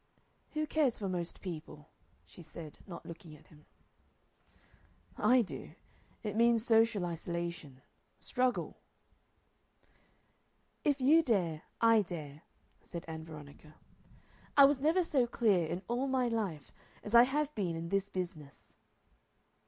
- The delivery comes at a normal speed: No, slow, 130 wpm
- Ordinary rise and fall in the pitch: No, wide, 6.9 semitones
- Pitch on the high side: Yes, high, 195 Hz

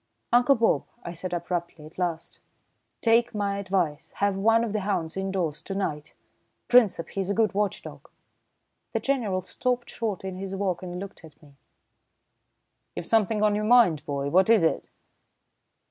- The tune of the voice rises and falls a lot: No, average, 3.9 semitones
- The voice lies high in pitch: Yes, high, 195 Hz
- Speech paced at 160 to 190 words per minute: Yes, average, 165 wpm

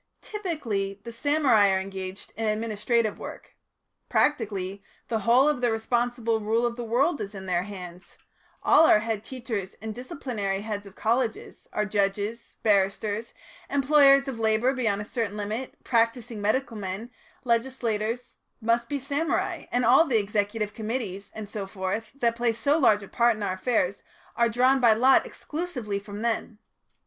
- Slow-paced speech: No, average, 160 wpm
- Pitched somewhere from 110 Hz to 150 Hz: No, high, 225 Hz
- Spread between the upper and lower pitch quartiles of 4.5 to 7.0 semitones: No, average, 3.3 semitones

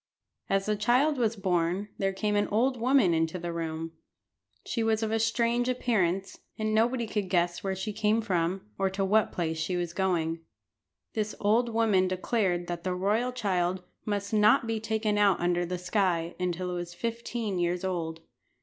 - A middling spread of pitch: Yes, average, 3.9 semitones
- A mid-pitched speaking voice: No, high, 195 Hz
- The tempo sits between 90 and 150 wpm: No, average, 180 wpm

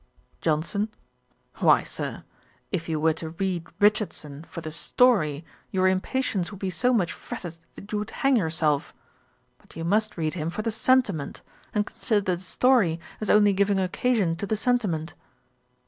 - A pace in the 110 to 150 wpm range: No, average, 160 wpm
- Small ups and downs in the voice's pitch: No, average, 4.5 semitones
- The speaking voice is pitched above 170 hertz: Yes, high, 190 Hz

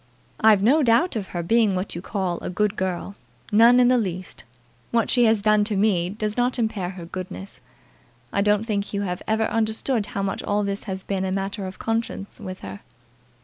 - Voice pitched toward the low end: No, high, 205 Hz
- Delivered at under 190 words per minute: No, fast, 205 wpm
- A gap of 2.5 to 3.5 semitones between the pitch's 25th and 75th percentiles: Yes, average, 2.9 semitones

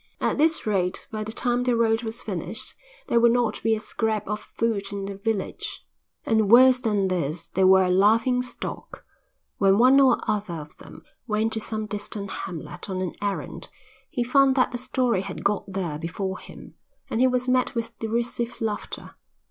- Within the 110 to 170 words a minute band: No, average, 190 wpm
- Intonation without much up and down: No, average, 3.5 semitones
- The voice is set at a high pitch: Yes, high, 220 Hz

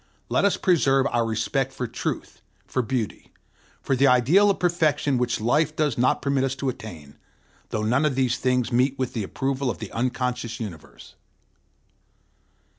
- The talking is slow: No, average, 165 wpm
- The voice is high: No, low, 130 Hz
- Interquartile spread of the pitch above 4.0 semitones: No, average, 2.8 semitones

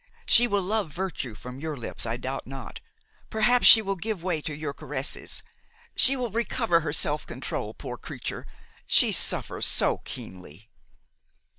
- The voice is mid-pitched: Yes, medium, 160 Hz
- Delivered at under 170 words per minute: Yes, average, 155 wpm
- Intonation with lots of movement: Yes, wide, 8.1 semitones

